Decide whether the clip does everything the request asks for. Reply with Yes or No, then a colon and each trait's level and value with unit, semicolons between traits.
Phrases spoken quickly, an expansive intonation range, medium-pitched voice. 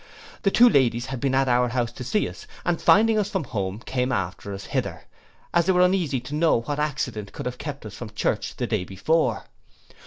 No: fast, 220 wpm; wide, 6.0 semitones; low, 130 Hz